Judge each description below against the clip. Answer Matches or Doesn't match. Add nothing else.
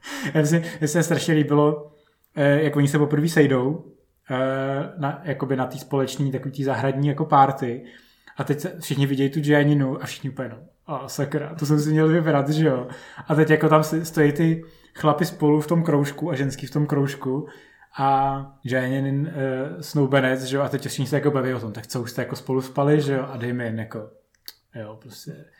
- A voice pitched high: Doesn't match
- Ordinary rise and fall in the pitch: Doesn't match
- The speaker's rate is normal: Doesn't match